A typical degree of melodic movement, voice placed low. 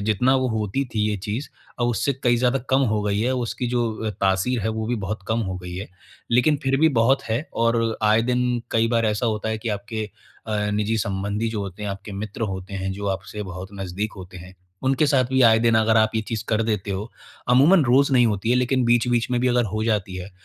Yes: average, 3.2 semitones; low, 110 Hz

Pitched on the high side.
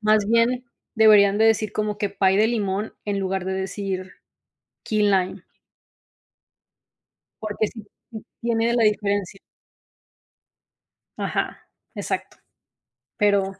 Yes: high, 205 Hz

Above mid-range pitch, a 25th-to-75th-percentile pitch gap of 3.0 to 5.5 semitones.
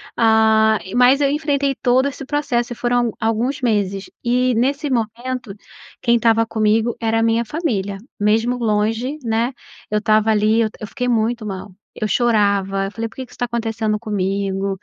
No: high, 225 Hz; narrow, 2.5 semitones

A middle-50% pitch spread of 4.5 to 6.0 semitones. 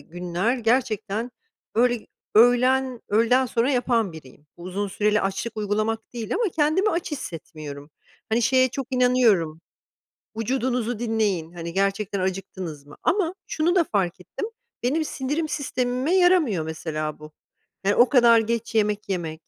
Yes: wide, 5.4 semitones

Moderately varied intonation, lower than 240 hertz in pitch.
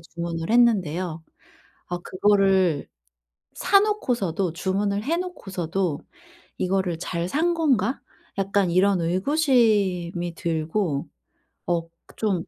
Yes: average, 4.0 semitones; high, 190 Hz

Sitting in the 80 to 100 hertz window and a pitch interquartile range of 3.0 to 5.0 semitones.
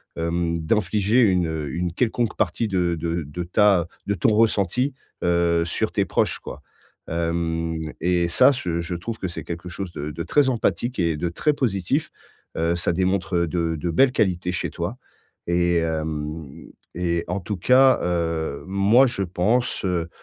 Yes: very low, 85 Hz; average, 3.3 semitones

